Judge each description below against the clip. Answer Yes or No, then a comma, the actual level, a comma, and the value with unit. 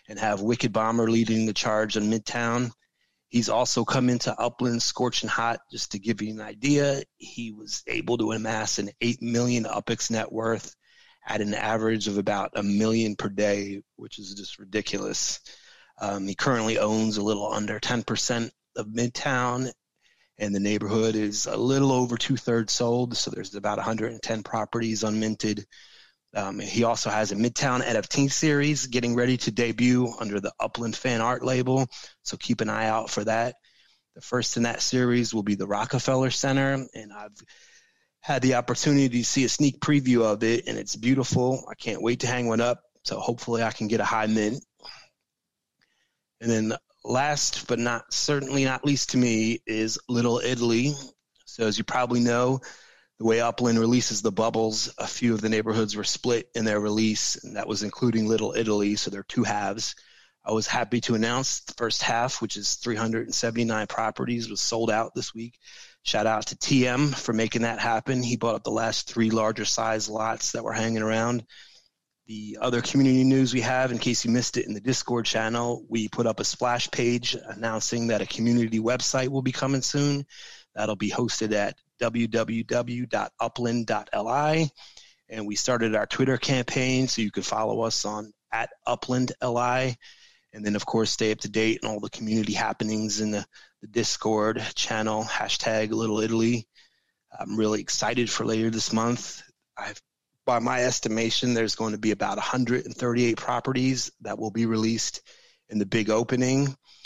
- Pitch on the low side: Yes, low, 115 Hz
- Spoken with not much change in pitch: Yes, narrow, 2.2 semitones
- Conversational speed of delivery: Yes, average, 175 wpm